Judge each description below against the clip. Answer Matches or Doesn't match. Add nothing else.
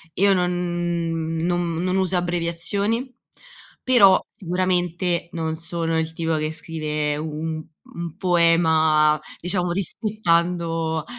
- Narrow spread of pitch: Matches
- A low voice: Doesn't match